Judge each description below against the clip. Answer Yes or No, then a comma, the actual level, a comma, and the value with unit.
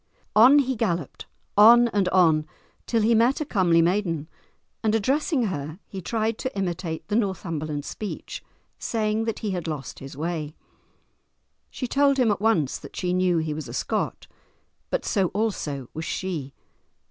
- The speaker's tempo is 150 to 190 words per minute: Yes, average, 160 wpm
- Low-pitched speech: No, high, 190 Hz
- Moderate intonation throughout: No, wide, 5.8 semitones